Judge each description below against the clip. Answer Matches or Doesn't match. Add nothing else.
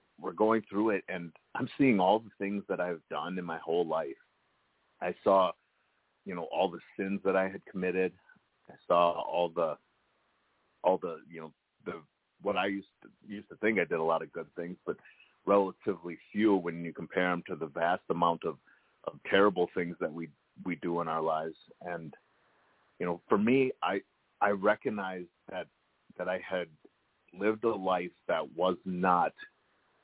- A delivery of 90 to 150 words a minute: Doesn't match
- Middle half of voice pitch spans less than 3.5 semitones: Matches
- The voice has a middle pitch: Doesn't match